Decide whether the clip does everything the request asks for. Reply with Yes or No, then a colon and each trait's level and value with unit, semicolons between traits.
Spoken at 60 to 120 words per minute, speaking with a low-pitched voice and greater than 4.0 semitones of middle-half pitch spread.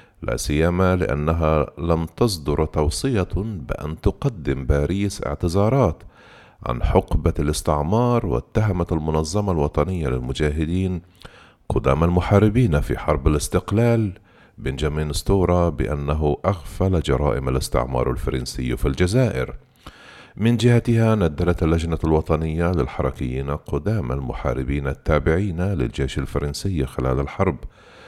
Yes: average, 95 wpm; very low, 80 Hz; average, 4.7 semitones